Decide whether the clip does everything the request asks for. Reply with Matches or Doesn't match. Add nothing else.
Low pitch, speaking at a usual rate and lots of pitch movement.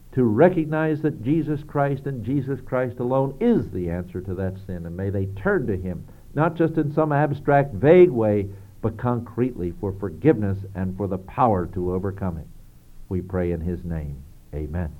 Matches